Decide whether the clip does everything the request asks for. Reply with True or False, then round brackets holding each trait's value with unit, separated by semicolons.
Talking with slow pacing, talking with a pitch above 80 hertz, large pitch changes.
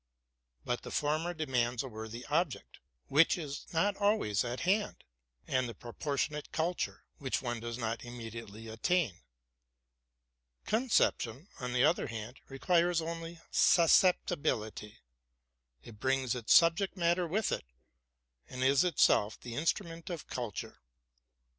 True (130 wpm; 140 Hz; 6.2 semitones)